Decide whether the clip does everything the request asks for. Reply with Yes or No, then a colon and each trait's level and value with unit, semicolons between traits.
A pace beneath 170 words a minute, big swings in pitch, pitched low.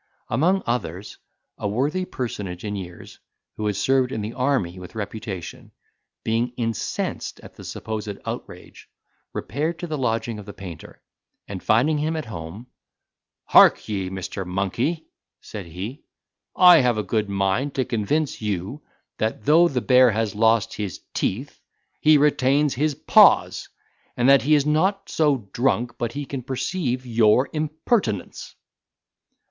Yes: average, 145 wpm; wide, 5.9 semitones; low, 120 Hz